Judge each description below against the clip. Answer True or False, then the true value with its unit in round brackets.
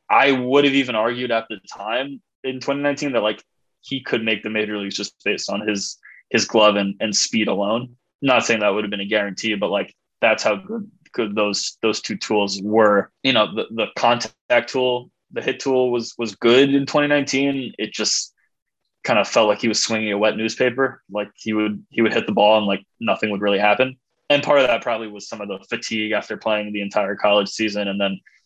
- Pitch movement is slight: False (3.8 semitones)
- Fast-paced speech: True (220 wpm)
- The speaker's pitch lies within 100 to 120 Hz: True (110 Hz)